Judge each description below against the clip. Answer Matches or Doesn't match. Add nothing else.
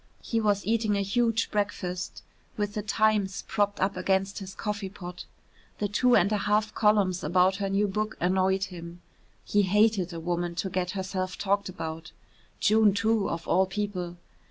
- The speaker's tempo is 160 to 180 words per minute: Matches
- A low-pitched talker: Doesn't match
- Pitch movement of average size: Doesn't match